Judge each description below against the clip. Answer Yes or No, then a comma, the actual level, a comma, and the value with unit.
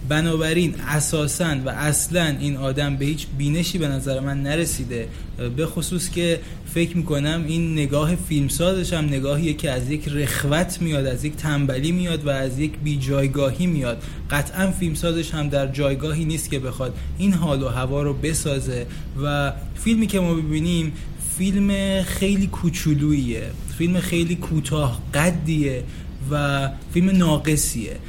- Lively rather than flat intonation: No, average, 3.3 semitones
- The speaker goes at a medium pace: Yes, average, 145 wpm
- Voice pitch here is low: No, medium, 150 Hz